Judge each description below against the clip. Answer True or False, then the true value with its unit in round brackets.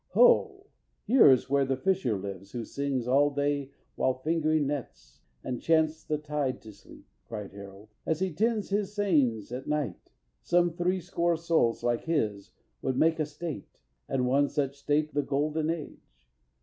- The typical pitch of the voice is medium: True (145 Hz)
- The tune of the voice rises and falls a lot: False (4.5 semitones)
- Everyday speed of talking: True (165 wpm)